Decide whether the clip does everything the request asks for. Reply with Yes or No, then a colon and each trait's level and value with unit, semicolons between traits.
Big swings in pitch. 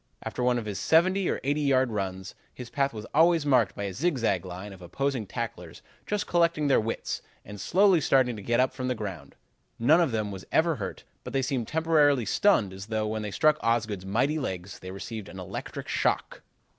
Yes: wide, 6.3 semitones